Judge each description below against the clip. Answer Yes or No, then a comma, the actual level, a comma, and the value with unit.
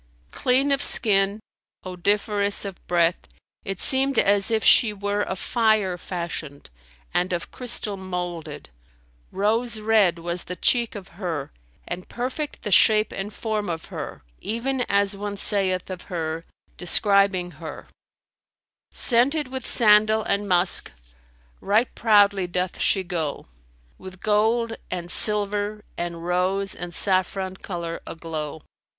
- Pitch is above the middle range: Yes, high, 195 Hz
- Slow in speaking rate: Yes, slow, 130 wpm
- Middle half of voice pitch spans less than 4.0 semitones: Yes, average, 3.4 semitones